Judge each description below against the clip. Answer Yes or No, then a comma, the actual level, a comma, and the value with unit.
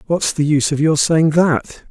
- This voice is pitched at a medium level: Yes, medium, 155 Hz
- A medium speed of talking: No, fast, 220 wpm